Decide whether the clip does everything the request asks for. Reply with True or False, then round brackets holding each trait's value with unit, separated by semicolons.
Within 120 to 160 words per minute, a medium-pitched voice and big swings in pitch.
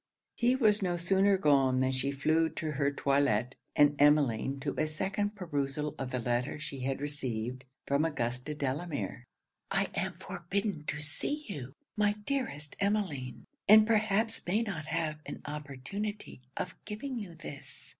True (155 wpm; 150 Hz; 6.5 semitones)